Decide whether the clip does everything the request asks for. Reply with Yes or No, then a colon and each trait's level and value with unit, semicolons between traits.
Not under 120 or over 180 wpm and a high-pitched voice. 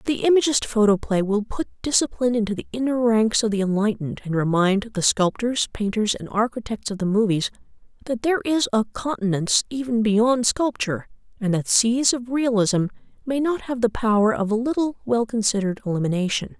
Yes: average, 170 wpm; high, 225 Hz